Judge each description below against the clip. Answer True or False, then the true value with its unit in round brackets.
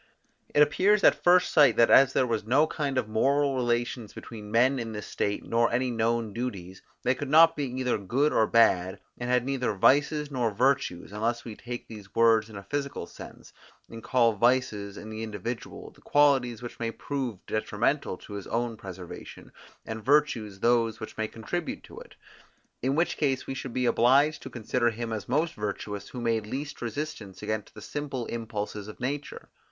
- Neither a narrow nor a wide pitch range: True (3.9 semitones)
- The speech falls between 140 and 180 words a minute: False (190 wpm)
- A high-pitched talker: False (120 Hz)